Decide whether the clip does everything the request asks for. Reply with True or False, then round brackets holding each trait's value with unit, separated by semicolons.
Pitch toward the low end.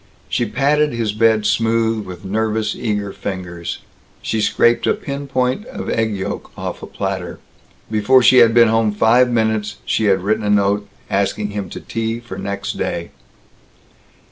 True (110 Hz)